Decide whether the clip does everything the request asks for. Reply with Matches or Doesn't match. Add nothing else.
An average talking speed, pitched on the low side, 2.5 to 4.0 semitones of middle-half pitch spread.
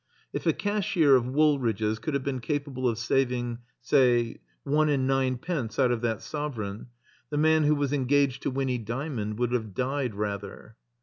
Matches